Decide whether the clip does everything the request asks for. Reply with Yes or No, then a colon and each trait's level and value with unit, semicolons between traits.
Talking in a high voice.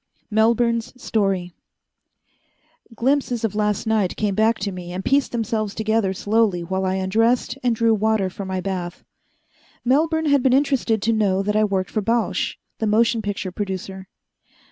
Yes: high, 215 Hz